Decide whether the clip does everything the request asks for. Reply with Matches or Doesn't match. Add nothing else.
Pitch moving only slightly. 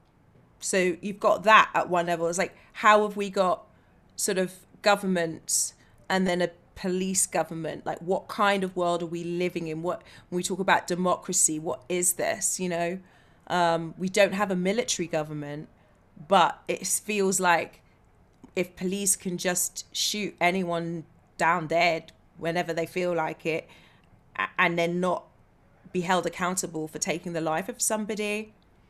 Matches